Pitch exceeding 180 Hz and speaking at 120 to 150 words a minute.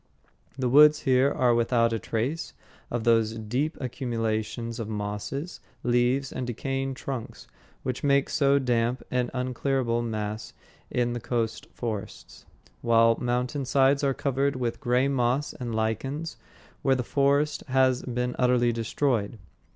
No: low, 125 Hz; slow, 135 wpm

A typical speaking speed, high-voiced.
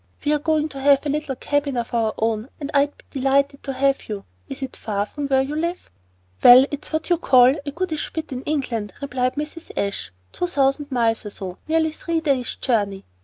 No: fast, 215 wpm; very high, 275 Hz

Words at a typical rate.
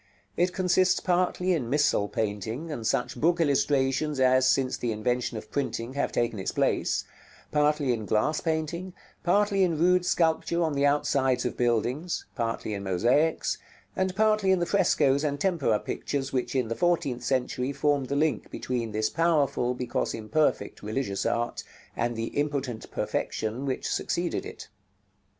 Yes: average, 155 wpm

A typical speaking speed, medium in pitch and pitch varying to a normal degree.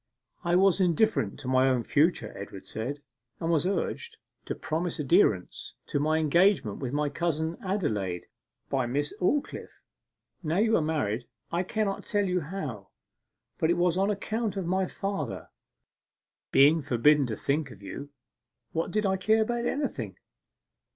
No: average, 155 wpm; medium, 160 Hz; wide, 6.2 semitones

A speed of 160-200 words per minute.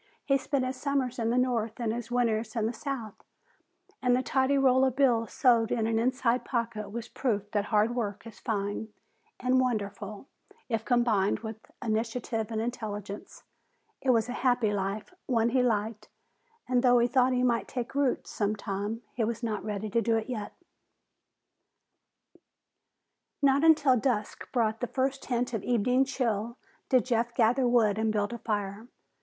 Yes: average, 170 wpm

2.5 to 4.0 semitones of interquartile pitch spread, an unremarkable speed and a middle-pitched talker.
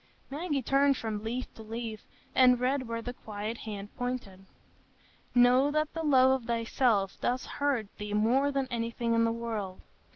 No: average, 3.0 semitones; average, 165 wpm; high, 235 Hz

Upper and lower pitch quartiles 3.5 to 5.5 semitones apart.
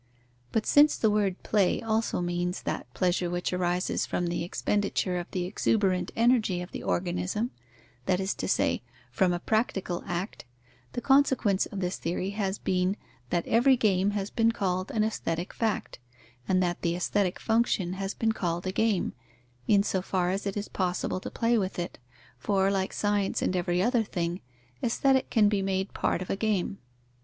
No: average, 3.1 semitones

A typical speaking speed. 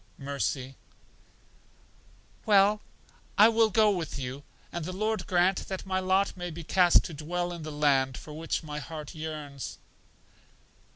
Yes: average, 150 wpm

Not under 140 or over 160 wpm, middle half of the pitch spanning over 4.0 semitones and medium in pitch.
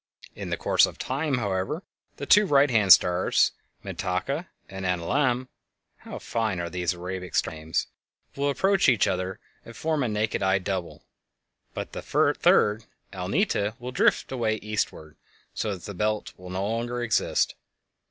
No: average, 155 wpm; average, 5.3 semitones; low, 105 Hz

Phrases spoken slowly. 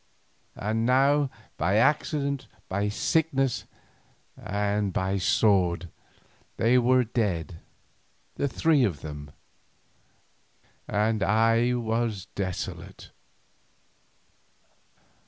Yes: slow, 80 wpm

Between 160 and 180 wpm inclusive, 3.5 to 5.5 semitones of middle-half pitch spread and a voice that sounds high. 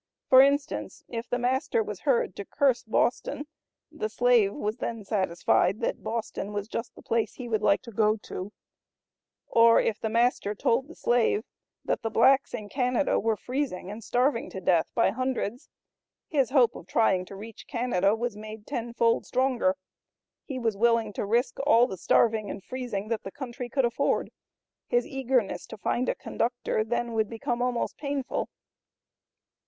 No: average, 170 wpm; average, 3.0 semitones; high, 235 Hz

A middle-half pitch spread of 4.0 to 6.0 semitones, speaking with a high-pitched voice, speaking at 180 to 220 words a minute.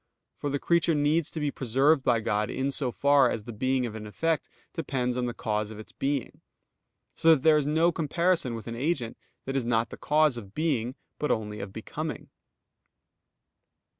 No: average, 4.7 semitones; low, 135 Hz; average, 195 wpm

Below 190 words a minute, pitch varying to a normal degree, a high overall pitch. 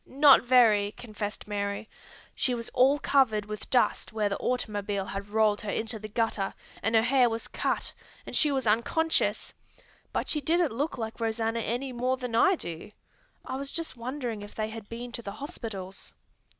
Yes: average, 180 wpm; average, 3.4 semitones; high, 230 Hz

